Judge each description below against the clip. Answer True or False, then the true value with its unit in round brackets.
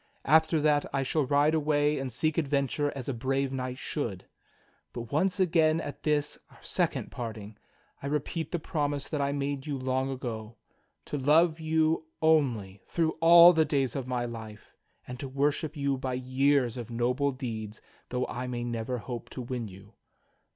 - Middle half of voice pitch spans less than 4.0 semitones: True (3.5 semitones)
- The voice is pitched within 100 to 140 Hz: True (135 Hz)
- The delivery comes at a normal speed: True (180 wpm)